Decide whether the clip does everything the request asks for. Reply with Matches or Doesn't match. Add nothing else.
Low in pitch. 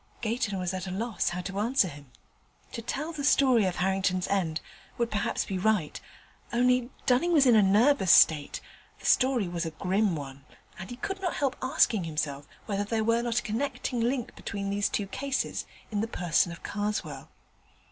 Doesn't match